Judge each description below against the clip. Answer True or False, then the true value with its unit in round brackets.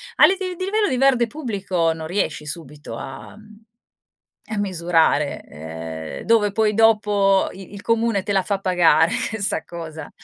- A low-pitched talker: False (195 Hz)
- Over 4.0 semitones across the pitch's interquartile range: True (5.6 semitones)